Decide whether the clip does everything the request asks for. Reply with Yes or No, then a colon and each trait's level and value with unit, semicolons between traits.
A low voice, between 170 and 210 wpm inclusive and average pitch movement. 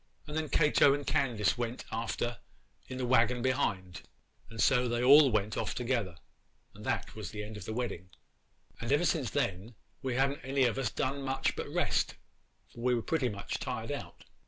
Yes: low, 125 Hz; average, 190 wpm; average, 3.5 semitones